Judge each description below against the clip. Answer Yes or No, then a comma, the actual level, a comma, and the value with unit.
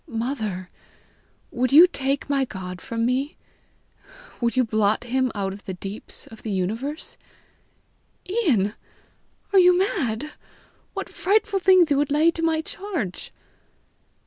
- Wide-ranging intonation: Yes, wide, 7.1 semitones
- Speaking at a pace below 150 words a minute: Yes, slow, 135 wpm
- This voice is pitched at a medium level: No, very high, 260 Hz